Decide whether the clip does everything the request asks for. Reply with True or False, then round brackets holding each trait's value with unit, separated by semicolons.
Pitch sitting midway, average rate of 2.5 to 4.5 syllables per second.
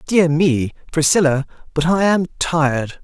True (160 Hz; 4.3 syllables/s)